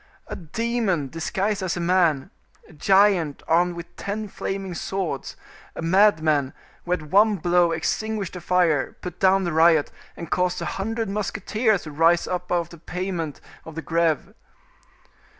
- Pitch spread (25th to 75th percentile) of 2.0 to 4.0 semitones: Yes, average, 3.1 semitones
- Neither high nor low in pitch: Yes, medium, 175 Hz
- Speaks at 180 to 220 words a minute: No, average, 155 wpm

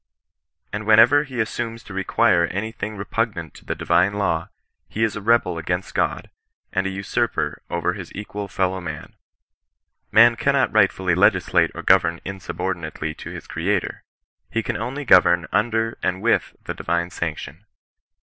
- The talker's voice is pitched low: Yes, low, 100 Hz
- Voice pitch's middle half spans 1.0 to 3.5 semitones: No, average, 4.1 semitones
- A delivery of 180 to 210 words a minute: No, average, 160 wpm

